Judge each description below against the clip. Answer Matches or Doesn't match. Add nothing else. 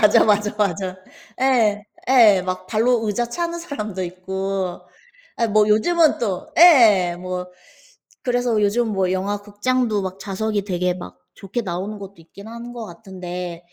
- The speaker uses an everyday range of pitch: Matches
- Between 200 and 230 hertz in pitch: Matches